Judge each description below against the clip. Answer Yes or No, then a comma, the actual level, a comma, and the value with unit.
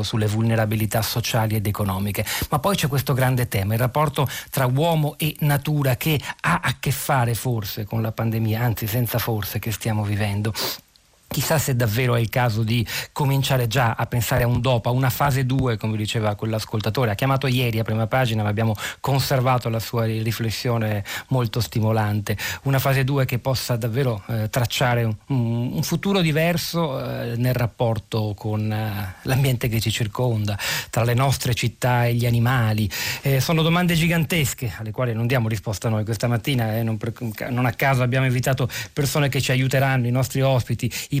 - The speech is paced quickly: Yes, fast, 180 wpm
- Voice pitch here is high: No, low, 120 Hz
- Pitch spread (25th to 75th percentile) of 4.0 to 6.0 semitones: No, average, 3.2 semitones